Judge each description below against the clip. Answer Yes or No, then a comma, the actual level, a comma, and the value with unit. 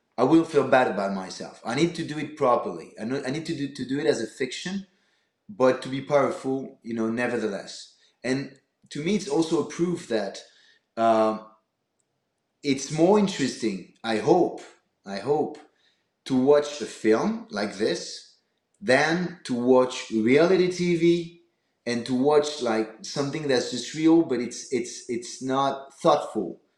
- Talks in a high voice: No, medium, 140 Hz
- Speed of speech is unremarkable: Yes, average, 155 wpm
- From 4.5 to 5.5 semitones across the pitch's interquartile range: Yes, average, 5.2 semitones